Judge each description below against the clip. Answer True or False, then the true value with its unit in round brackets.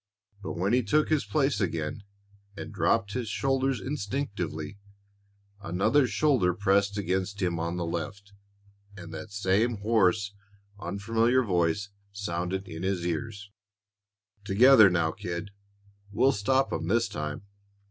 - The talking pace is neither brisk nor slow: False (125 wpm)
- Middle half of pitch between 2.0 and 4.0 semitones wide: False (4.6 semitones)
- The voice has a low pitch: True (100 Hz)